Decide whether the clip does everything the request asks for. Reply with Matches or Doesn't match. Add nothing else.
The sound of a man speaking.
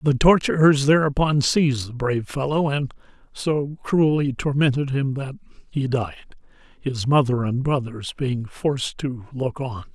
Matches